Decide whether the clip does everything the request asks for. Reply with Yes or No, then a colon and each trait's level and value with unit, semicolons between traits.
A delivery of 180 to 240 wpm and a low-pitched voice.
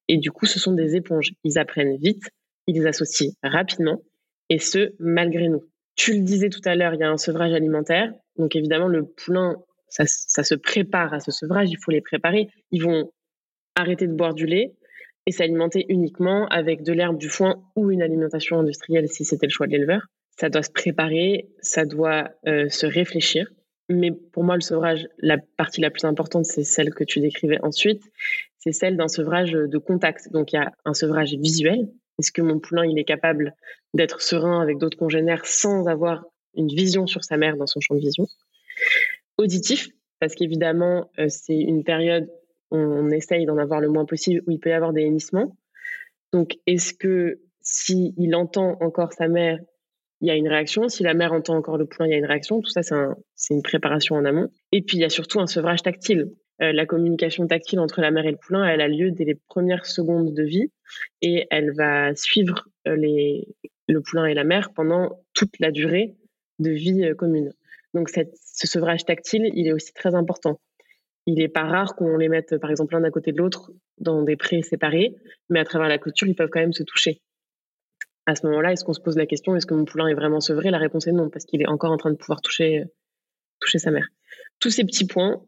No: average, 215 wpm; medium, 165 Hz